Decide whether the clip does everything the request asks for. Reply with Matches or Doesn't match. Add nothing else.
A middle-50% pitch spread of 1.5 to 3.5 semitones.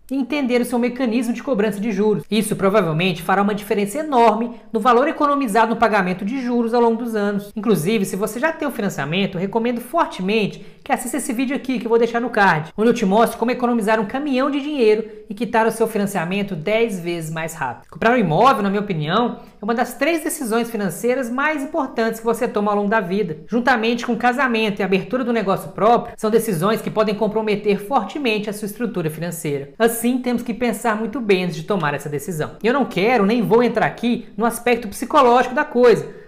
Matches